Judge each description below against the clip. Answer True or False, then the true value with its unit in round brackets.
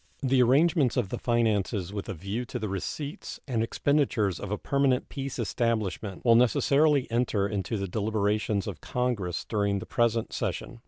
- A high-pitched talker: False (115 Hz)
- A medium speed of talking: True (165 wpm)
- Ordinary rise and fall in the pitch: True (3.8 semitones)